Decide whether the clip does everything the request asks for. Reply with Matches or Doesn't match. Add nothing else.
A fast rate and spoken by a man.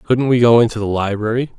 Matches